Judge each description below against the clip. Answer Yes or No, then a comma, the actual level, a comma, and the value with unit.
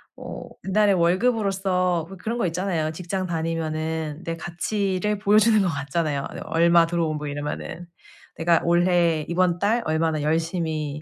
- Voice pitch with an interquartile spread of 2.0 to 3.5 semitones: Yes, average, 2.9 semitones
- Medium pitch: Yes, medium, 170 Hz